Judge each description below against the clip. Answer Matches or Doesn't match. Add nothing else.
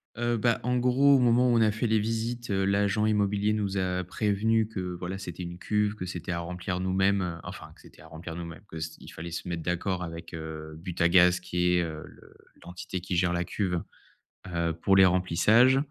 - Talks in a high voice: Doesn't match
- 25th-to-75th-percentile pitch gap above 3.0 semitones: Matches